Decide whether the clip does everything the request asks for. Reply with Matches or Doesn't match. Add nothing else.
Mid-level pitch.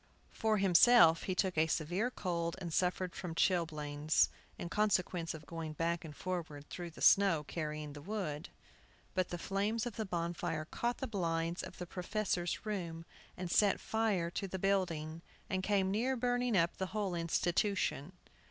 Matches